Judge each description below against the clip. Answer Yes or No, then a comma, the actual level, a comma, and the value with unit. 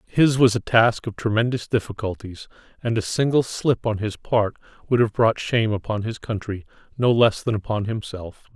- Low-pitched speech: Yes, low, 110 Hz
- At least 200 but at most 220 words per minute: No, average, 180 wpm